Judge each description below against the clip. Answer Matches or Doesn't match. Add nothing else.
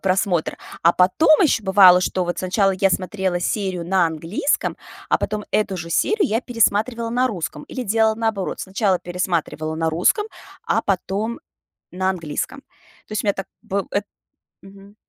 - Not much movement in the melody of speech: Doesn't match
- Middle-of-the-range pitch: Doesn't match